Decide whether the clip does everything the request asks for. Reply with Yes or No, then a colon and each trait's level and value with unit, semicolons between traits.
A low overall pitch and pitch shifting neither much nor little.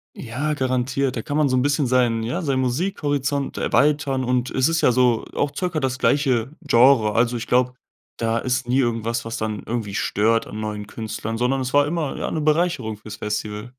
Yes: low, 125 Hz; average, 3.8 semitones